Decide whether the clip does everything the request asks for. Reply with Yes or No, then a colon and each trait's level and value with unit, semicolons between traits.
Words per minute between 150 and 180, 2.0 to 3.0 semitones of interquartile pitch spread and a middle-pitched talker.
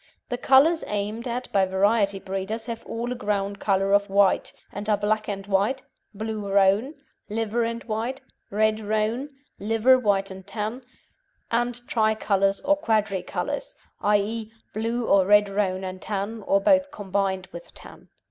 No: average, 155 wpm; average, 2.7 semitones; high, 210 Hz